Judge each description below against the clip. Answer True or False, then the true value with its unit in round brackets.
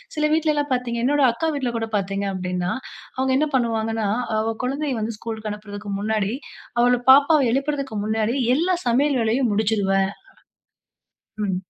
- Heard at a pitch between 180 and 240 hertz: True (230 Hz)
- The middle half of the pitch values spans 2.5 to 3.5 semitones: False (4.5 semitones)